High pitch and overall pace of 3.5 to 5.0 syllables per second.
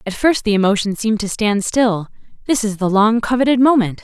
No: high, 220 Hz; 5.4 syllables/s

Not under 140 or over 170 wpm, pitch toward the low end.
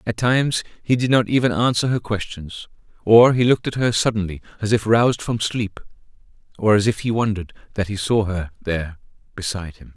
No: average, 195 wpm; low, 110 Hz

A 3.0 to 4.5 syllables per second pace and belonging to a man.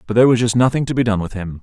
No: 8.1 syllables/s; male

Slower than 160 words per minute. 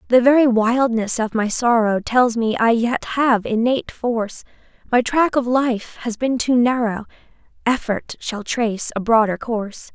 No: average, 165 wpm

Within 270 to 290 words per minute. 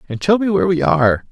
Yes: fast, 275 wpm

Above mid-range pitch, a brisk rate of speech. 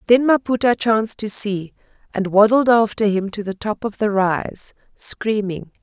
No: high, 210 Hz; average, 165 wpm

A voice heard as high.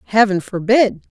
Yes: high, 210 Hz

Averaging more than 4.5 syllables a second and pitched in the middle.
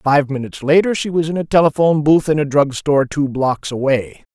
Yes: 5.7 syllables/s; medium, 145 Hz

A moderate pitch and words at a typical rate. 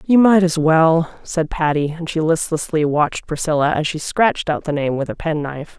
No: medium, 160 Hz; fast, 210 wpm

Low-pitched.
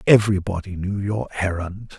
Yes: low, 100 Hz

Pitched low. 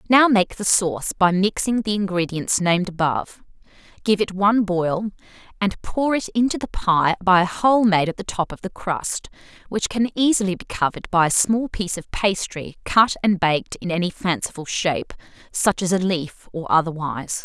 No: high, 190 Hz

